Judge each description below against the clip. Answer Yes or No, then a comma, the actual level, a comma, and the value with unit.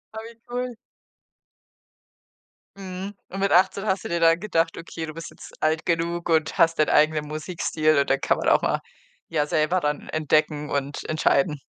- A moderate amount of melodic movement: Yes, average, 3.1 semitones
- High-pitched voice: No, medium, 165 Hz